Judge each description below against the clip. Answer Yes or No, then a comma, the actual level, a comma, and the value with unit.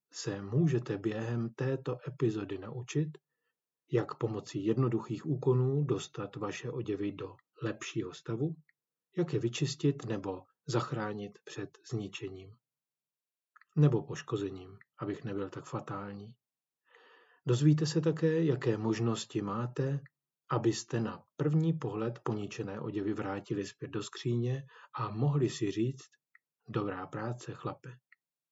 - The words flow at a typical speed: No, slow, 110 wpm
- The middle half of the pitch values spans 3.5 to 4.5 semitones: No, average, 5.0 semitones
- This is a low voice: Yes, low, 120 Hz